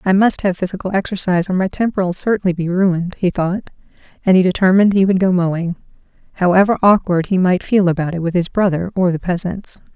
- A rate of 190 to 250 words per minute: Yes, average, 200 wpm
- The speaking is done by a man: No, female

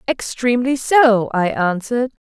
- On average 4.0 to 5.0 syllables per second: Yes, 4.6 syllables/s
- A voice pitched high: Yes, high, 235 Hz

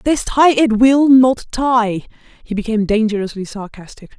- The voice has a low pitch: No, high, 230 Hz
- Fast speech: No, average, 145 wpm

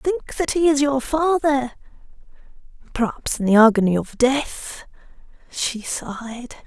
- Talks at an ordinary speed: No, slow, 125 wpm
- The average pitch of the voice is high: Yes, very high, 265 Hz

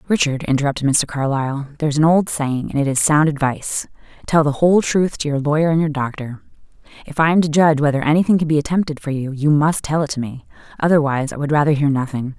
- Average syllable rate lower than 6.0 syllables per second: No, 6.5 syllables/s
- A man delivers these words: No, female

